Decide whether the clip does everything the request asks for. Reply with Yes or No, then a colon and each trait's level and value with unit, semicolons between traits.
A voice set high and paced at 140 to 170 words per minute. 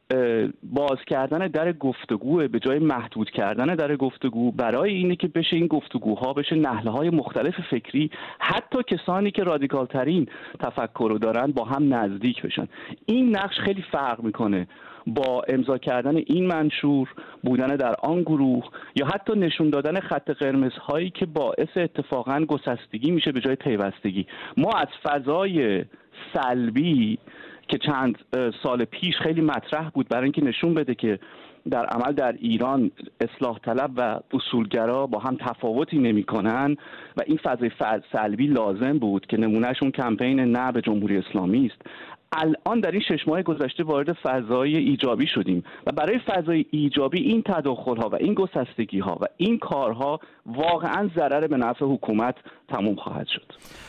No: medium, 140 Hz; fast, 155 wpm